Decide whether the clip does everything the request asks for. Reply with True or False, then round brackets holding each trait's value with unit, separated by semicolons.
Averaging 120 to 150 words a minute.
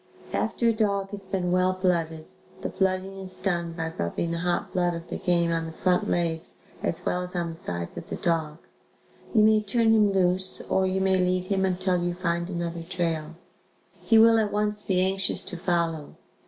False (200 wpm)